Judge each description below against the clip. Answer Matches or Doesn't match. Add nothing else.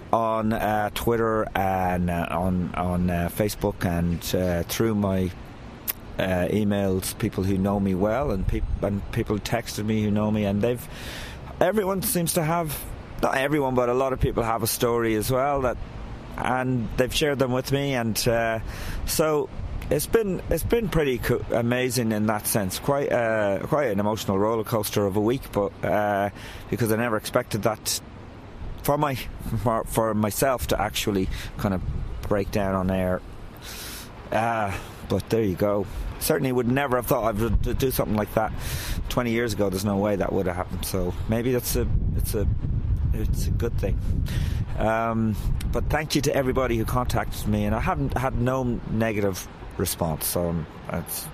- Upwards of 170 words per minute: Matches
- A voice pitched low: Matches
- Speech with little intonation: Doesn't match